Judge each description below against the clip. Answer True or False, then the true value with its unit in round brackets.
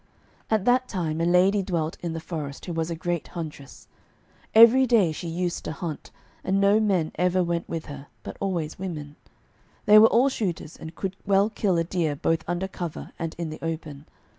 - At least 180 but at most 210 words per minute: True (195 wpm)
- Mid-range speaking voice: True (175 Hz)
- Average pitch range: True (3.3 semitones)